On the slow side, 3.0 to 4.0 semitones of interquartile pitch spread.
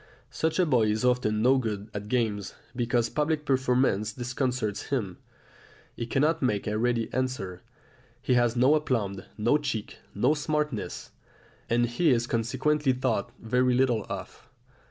No: average, 145 wpm; average, 3.3 semitones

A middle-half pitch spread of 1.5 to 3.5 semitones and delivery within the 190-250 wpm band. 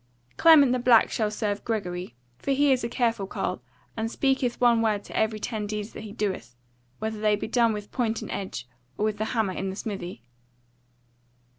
Yes: narrow, 2.6 semitones; average, 195 wpm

